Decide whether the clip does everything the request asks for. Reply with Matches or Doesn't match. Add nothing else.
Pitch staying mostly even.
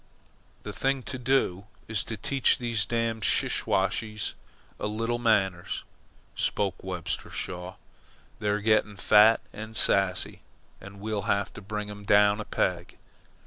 Matches